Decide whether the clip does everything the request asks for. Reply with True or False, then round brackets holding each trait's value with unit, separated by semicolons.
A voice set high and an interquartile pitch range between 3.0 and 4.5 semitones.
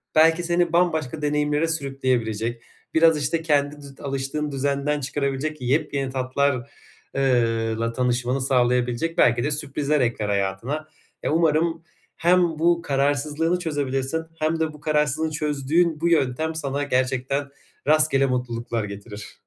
False (140 Hz; 3.6 semitones)